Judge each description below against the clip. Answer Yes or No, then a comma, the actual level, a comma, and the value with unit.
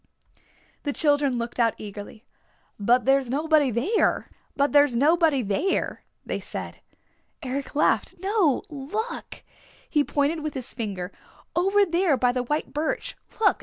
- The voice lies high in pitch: Yes, very high, 285 Hz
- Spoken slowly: Yes, slow, 120 wpm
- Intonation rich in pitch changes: No, average, 4.5 semitones